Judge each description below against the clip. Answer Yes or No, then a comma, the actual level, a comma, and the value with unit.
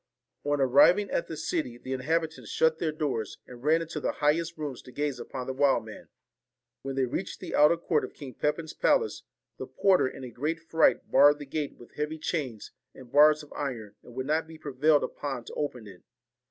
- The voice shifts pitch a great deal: No, average, 3.4 semitones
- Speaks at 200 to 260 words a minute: Yes, fast, 205 wpm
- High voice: No, medium, 145 Hz